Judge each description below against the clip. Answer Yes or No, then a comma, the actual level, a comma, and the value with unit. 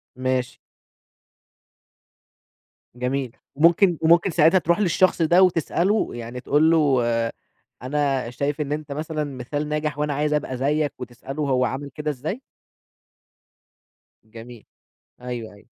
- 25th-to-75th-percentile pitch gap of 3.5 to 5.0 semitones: Yes, average, 3.8 semitones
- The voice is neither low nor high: Yes, medium, 145 Hz